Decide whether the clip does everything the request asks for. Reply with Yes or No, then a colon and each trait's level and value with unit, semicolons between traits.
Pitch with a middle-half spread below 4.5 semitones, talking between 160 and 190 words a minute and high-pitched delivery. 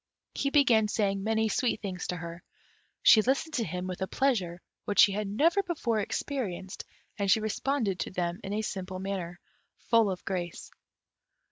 Yes: average, 3.9 semitones; average, 170 wpm; high, 200 Hz